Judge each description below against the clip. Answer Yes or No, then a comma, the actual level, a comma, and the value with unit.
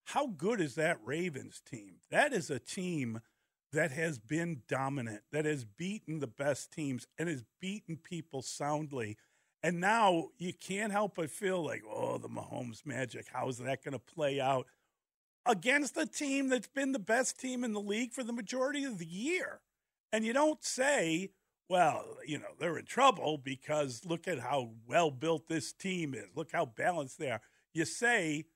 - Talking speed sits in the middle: Yes, average, 185 wpm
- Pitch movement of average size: No, wide, 7.2 semitones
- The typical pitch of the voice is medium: Yes, medium, 165 Hz